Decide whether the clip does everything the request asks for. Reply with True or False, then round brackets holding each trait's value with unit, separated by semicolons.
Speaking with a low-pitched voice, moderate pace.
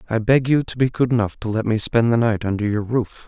False (115 Hz; 295 wpm)